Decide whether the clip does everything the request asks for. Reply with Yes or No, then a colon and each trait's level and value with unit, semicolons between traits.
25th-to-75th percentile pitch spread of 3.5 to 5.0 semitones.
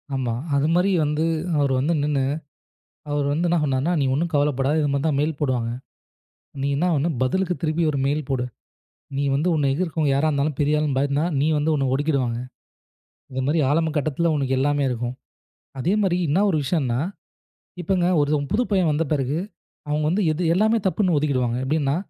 No: average, 2.9 semitones